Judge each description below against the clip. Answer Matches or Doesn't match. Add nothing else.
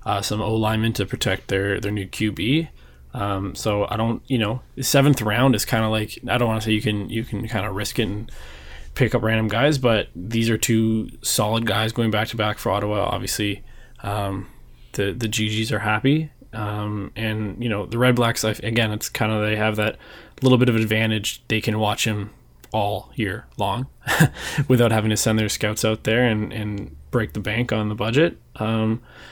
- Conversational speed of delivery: Doesn't match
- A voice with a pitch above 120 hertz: Doesn't match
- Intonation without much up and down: Matches